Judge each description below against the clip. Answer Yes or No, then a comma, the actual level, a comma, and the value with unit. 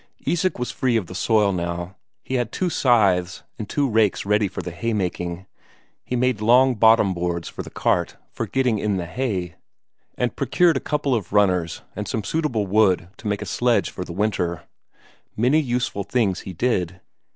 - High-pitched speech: No, low, 105 Hz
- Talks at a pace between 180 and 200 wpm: Yes, average, 185 wpm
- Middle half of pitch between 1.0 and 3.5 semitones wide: No, average, 5.2 semitones